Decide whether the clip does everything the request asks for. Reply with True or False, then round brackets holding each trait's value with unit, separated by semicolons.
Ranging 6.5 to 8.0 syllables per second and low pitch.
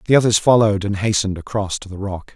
True (6.9 syllables/s; 100 Hz)